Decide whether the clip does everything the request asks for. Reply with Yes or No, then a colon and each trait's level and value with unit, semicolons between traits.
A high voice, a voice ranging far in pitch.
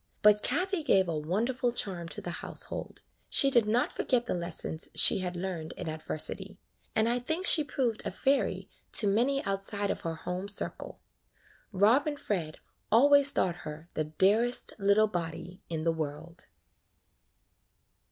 Yes: high, 200 Hz; wide, 6.2 semitones